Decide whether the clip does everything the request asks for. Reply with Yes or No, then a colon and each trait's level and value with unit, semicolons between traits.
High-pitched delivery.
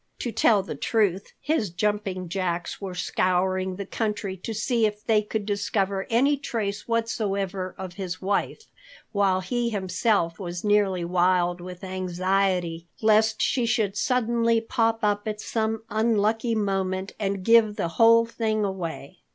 Yes: high, 200 Hz